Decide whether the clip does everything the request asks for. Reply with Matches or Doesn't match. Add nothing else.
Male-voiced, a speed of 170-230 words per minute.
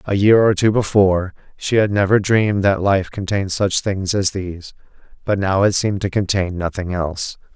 Matches